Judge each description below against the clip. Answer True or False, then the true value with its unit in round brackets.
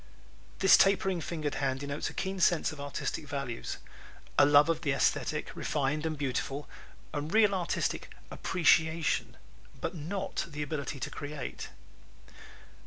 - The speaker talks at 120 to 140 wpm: True (135 wpm)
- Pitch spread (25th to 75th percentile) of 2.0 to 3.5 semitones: True (2.9 semitones)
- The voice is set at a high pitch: False (150 Hz)